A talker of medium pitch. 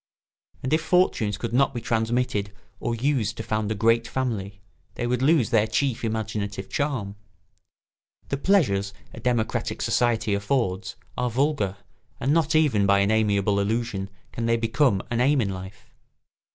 No: low, 115 Hz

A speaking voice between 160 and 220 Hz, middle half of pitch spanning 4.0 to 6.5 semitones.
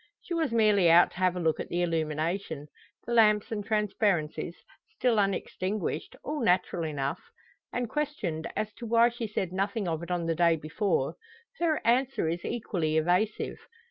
Yes: high, 190 Hz; average, 5.2 semitones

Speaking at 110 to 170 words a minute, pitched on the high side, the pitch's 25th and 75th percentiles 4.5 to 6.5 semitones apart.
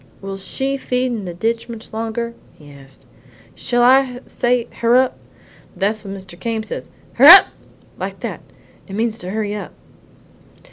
No: average, 155 wpm; high, 225 Hz; average, 3.9 semitones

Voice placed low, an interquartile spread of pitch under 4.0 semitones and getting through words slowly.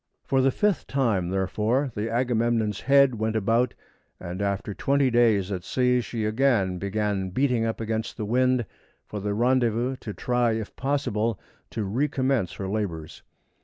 No: low, 115 Hz; average, 3.6 semitones; average, 155 wpm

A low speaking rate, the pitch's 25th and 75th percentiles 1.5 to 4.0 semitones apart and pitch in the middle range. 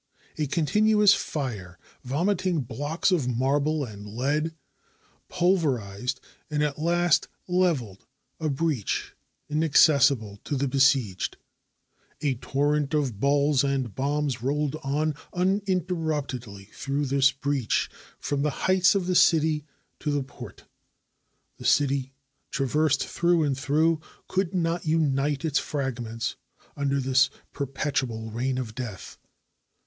Yes: slow, 115 wpm; average, 3.4 semitones; medium, 145 Hz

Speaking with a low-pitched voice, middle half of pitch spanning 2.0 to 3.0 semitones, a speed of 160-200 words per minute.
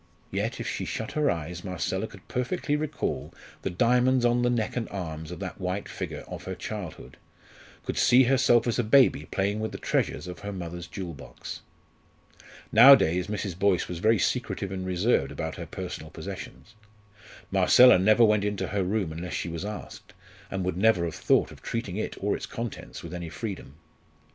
No: low, 100 Hz; average, 4.7 semitones; average, 185 wpm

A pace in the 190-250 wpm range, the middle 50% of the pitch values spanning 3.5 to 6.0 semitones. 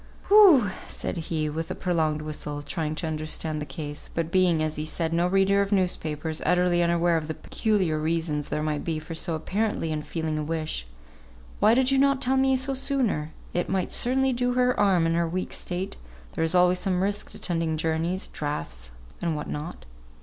Yes: average, 195 wpm; average, 3.9 semitones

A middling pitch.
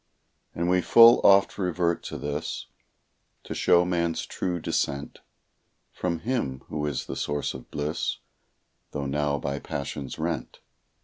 No: very low, 80 Hz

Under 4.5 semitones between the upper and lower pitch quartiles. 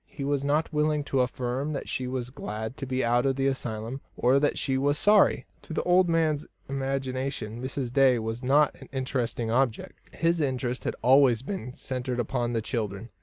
Yes: narrow, 2.6 semitones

